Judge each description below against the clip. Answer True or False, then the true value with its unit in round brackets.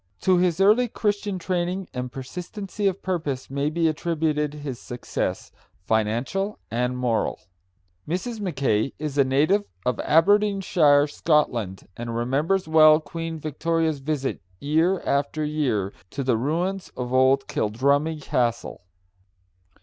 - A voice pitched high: False (150 Hz)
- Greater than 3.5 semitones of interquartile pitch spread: True (5.3 semitones)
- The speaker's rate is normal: False (125 wpm)